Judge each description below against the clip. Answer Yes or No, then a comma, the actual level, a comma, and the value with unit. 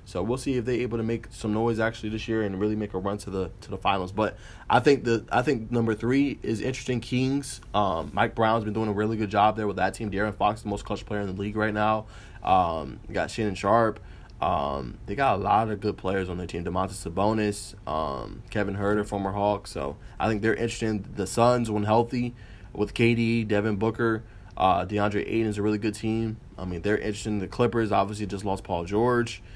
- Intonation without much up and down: Yes, narrow, 2.0 semitones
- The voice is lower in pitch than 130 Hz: Yes, low, 105 Hz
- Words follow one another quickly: Yes, fast, 230 wpm